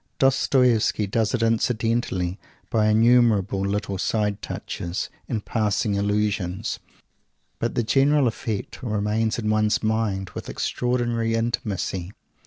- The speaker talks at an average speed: No, slow, 110 wpm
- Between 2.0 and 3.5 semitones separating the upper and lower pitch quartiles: Yes, narrow, 2.4 semitones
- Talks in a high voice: No, low, 110 Hz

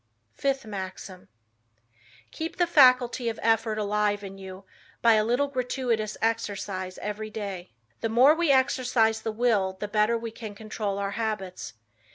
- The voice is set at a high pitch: Yes, high, 220 Hz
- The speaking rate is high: No, average, 150 wpm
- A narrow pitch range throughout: No, average, 3.1 semitones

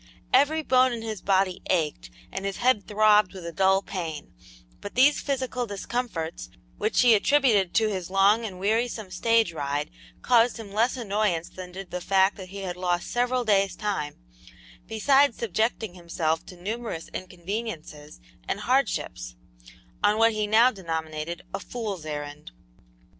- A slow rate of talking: No, average, 155 wpm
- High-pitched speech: Yes, high, 200 Hz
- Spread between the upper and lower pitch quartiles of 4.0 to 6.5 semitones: Yes, average, 4.4 semitones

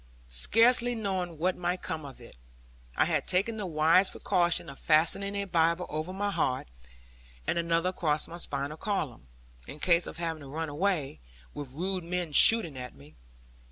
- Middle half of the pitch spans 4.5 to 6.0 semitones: No, average, 3.9 semitones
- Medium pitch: Yes, medium, 170 Hz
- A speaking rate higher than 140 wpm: Yes, average, 170 wpm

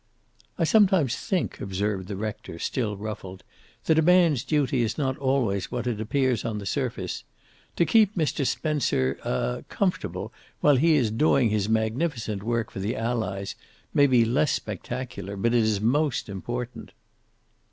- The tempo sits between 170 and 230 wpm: No, average, 155 wpm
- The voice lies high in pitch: No, low, 120 Hz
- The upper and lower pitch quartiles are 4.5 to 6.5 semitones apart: Yes, average, 5.3 semitones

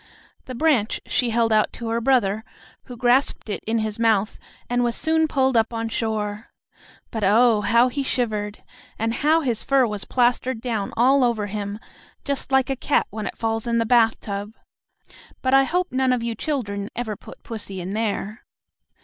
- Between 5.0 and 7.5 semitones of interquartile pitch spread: No, average, 3.1 semitones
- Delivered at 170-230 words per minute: Yes, average, 185 wpm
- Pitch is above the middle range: Yes, high, 230 Hz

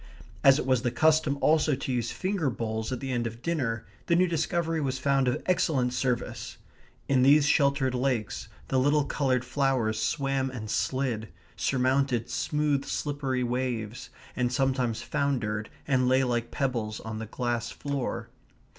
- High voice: No, low, 130 Hz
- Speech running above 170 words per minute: No, average, 155 wpm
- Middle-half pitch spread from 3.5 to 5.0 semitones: No, average, 2.8 semitones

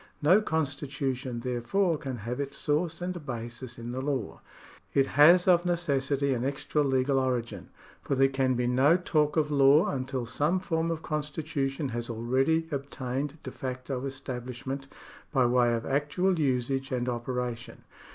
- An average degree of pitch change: Yes, average, 3.1 semitones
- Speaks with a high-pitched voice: No, low, 135 Hz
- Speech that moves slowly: No, average, 160 wpm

